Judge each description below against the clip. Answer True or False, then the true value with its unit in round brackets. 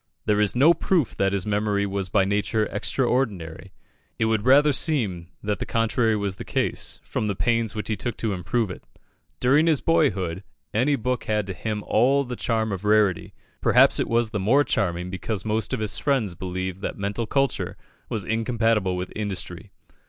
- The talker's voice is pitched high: False (105 Hz)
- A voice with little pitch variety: False (3.6 semitones)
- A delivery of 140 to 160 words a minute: False (185 wpm)